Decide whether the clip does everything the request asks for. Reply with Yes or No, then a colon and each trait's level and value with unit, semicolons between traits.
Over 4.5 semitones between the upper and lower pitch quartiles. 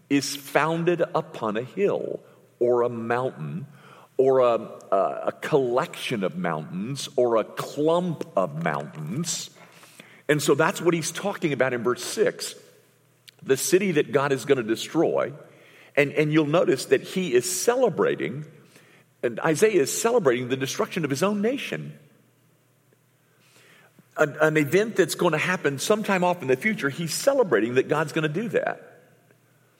Yes: average, 5.0 semitones